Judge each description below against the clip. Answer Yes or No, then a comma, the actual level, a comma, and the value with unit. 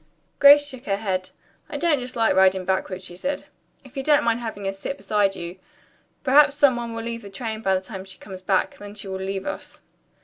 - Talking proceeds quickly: Yes, fast, 225 wpm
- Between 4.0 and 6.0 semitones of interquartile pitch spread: Yes, average, 5.2 semitones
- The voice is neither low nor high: No, high, 210 Hz